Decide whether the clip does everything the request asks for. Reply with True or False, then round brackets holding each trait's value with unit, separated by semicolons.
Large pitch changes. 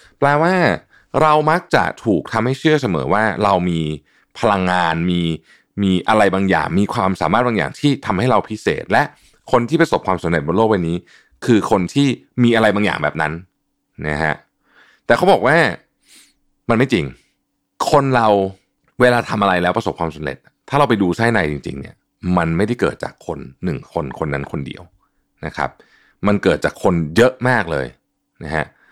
True (6.5 semitones)